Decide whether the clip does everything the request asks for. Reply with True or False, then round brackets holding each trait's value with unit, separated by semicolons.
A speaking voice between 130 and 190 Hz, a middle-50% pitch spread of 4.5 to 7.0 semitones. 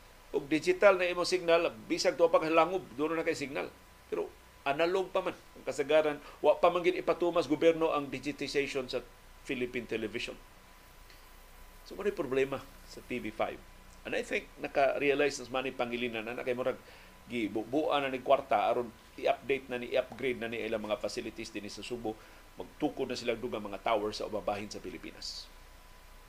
True (140 Hz; 5.4 semitones)